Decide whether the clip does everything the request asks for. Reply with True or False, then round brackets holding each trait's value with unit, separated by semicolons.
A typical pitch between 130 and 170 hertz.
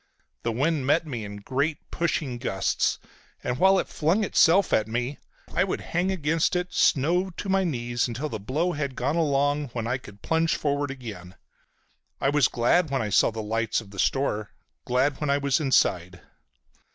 True (140 Hz)